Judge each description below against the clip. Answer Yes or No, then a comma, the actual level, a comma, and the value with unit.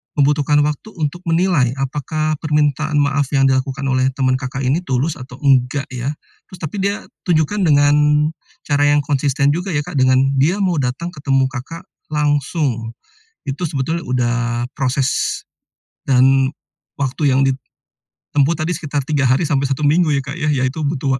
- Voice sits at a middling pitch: Yes, medium, 145 Hz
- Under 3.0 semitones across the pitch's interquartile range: Yes, narrow, 2.6 semitones